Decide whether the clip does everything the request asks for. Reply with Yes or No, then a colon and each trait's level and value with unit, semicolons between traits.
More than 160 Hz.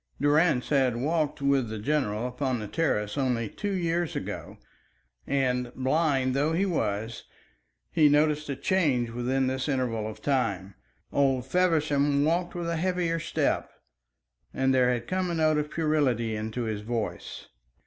No: low, 135 Hz